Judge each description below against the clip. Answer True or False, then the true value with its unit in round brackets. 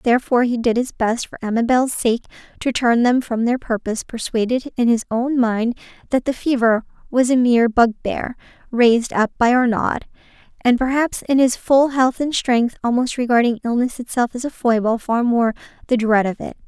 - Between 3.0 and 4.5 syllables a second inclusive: False (5.2 syllables/s)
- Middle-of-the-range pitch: False (240 Hz)